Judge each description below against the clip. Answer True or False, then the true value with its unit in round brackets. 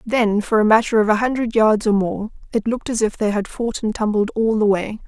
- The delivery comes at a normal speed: False (260 wpm)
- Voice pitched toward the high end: True (220 Hz)